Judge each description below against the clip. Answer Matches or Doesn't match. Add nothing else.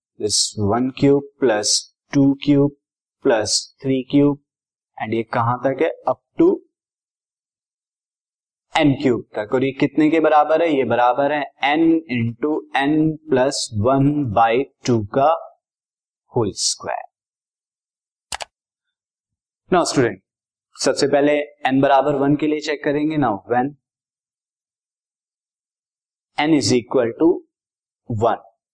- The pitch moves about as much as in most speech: Matches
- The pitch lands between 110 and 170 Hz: Matches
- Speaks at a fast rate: Doesn't match